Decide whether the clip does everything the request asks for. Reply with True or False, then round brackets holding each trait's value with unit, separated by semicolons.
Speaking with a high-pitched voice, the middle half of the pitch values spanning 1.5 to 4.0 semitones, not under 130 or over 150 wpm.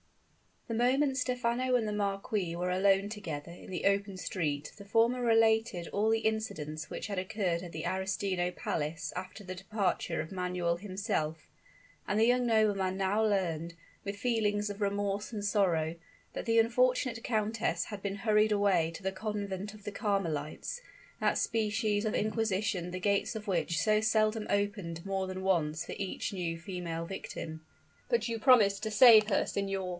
False (200 Hz; 3.2 semitones; 170 wpm)